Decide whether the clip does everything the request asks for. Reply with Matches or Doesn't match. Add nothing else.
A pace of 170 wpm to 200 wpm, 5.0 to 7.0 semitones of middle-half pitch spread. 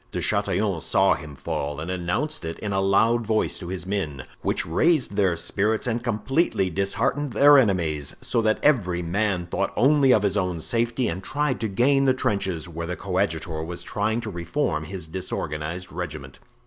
Matches